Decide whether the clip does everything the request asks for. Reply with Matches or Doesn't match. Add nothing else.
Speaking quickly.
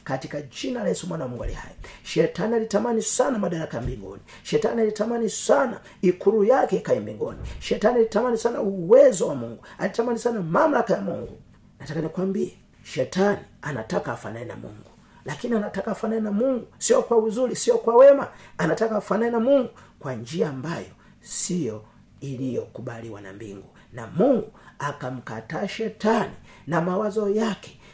Matches